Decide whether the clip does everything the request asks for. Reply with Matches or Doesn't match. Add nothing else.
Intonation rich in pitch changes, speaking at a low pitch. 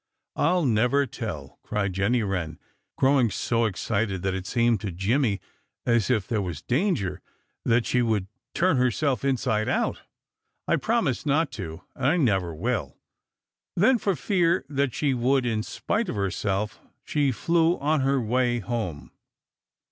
Matches